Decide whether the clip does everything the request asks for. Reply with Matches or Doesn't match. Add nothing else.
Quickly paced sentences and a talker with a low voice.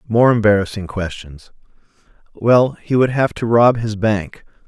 Doesn't match